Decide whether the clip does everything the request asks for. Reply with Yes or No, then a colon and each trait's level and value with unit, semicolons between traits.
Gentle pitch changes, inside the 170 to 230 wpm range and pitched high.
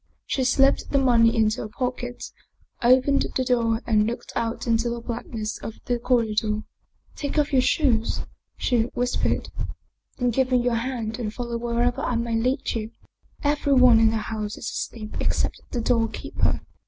Yes: narrow, 2.0 semitones; average, 175 wpm; high, 235 Hz